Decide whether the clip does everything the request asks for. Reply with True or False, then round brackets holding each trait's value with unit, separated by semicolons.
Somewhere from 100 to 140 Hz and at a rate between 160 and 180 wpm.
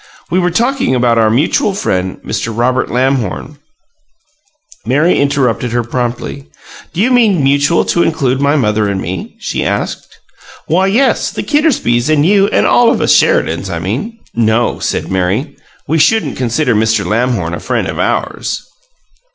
True (135 Hz; 165 wpm)